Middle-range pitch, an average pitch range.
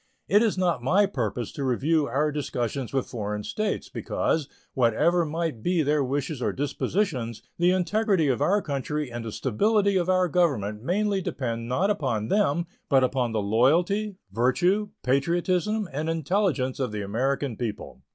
No: medium, 145 Hz; wide, 6.6 semitones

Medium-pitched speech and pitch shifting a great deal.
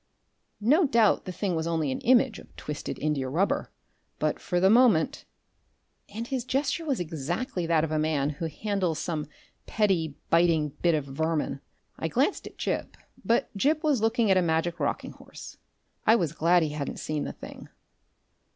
Yes: medium, 175 Hz; wide, 6.6 semitones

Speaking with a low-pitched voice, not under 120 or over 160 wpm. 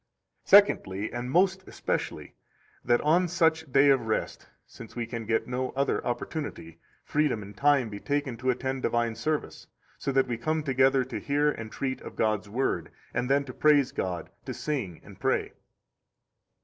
No: low, 130 Hz; average, 175 wpm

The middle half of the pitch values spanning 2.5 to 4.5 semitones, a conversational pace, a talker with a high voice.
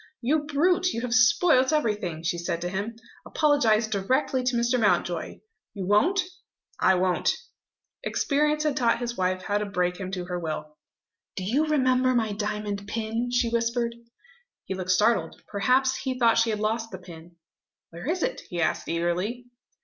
No: average, 5.3 semitones; average, 170 wpm; high, 225 Hz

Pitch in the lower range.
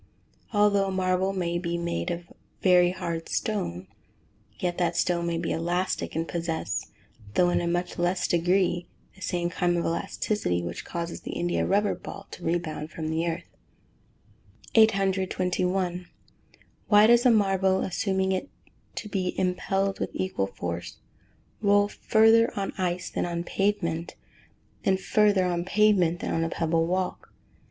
No: medium, 180 Hz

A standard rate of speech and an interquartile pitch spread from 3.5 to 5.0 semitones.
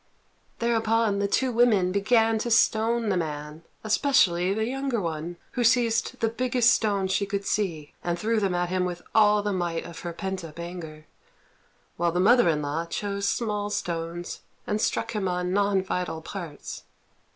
Yes: average, 175 wpm; average, 4.4 semitones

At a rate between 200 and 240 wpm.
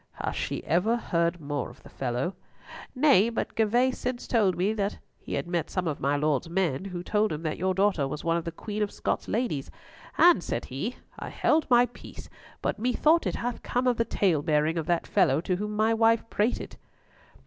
Yes: fast, 205 wpm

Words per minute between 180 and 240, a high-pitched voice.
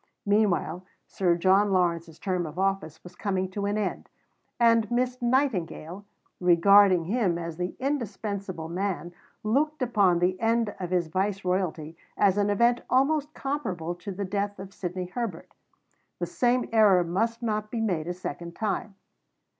No: average, 150 wpm; high, 195 Hz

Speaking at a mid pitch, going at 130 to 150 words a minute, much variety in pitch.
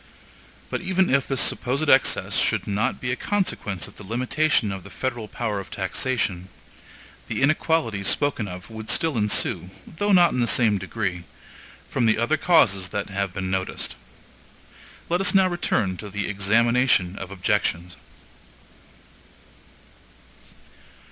No: low, 110 Hz; average, 140 wpm; wide, 6.0 semitones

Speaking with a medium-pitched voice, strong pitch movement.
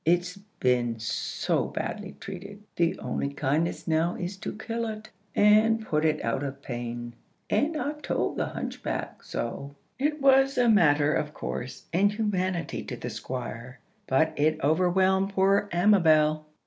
Yes: medium, 175 Hz; wide, 6.1 semitones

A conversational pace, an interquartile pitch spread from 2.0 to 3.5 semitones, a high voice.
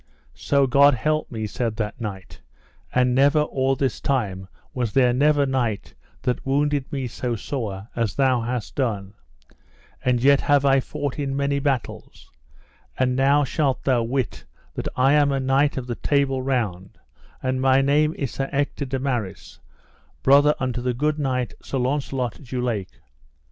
No: average, 165 wpm; narrow, 2.5 semitones; low, 130 Hz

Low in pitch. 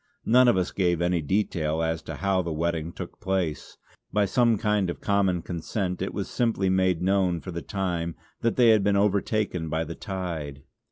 Yes: very low, 95 Hz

